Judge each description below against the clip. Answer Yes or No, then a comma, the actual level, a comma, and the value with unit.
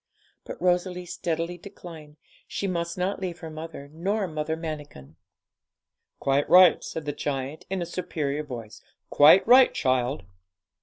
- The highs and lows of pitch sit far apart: No, average, 3.6 semitones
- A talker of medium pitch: Yes, medium, 160 Hz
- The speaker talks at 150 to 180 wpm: No, average, 140 wpm